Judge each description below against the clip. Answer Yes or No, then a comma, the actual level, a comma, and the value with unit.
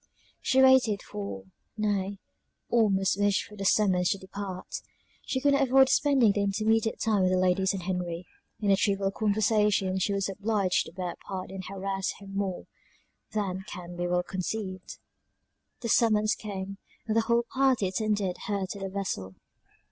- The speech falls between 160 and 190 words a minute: Yes, average, 170 wpm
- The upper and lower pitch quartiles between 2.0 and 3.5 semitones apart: Yes, narrow, 2.4 semitones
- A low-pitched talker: No, high, 195 Hz